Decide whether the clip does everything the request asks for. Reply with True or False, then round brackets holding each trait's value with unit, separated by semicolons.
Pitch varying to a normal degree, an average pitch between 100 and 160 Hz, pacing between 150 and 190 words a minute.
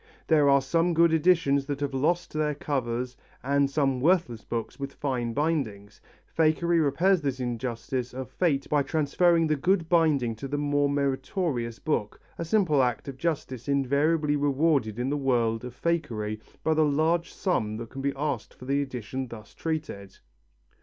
True (3.9 semitones; 140 Hz; 165 wpm)